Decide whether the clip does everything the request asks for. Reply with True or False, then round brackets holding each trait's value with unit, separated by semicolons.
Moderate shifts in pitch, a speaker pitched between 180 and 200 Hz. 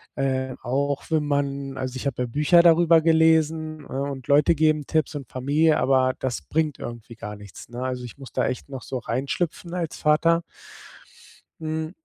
False (3.4 semitones; 140 Hz)